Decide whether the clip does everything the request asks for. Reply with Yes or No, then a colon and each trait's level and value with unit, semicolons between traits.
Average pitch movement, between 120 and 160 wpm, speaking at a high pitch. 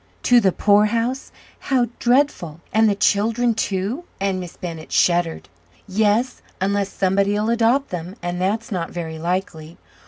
Yes: average, 4.3 semitones; slow, 135 wpm; high, 200 Hz